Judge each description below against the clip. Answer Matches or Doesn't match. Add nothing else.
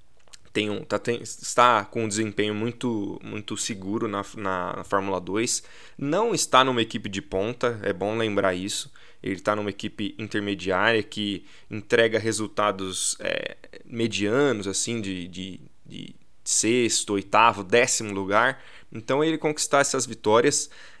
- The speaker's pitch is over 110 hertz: Doesn't match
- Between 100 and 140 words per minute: Matches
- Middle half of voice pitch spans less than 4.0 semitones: Matches